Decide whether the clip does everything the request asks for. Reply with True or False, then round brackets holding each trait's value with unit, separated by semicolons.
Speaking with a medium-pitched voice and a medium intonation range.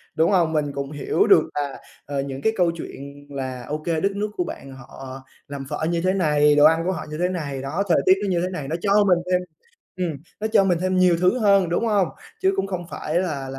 True (165 Hz; 4.7 semitones)